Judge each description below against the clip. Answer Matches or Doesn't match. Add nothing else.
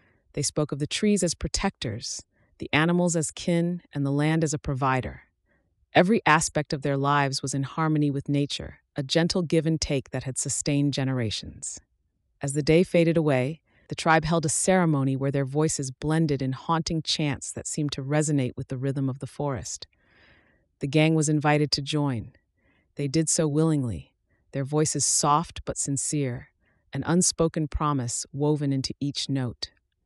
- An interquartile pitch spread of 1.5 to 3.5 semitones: Matches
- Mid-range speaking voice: Matches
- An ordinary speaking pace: Matches